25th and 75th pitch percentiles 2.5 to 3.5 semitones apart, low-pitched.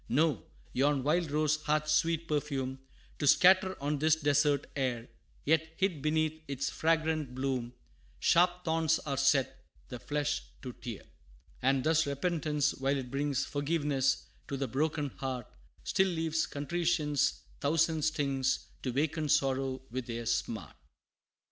No: average, 3.0 semitones; medium, 145 Hz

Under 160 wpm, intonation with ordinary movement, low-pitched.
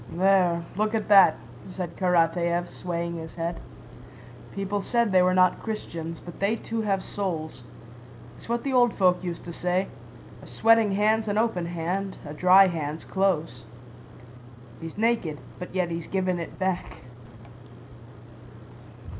No: average, 145 wpm; average, 3.1 semitones; medium, 185 Hz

